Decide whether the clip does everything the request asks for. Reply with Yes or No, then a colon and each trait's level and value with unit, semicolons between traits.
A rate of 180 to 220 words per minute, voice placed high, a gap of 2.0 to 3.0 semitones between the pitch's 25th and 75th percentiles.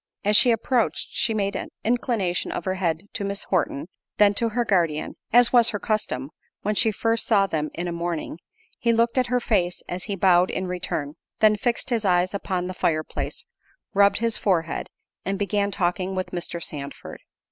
No: average, 190 wpm; high, 195 Hz; average, 4.0 semitones